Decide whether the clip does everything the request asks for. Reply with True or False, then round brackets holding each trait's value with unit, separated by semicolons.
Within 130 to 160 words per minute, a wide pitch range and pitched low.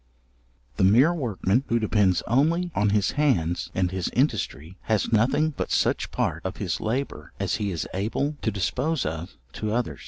False (175 wpm; 6.1 semitones; 110 Hz)